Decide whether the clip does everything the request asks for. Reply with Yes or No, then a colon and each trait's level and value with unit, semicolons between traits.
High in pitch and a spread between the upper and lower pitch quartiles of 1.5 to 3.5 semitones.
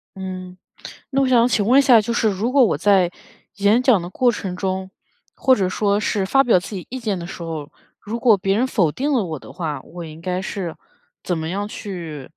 No: high, 195 Hz; average, 4.6 semitones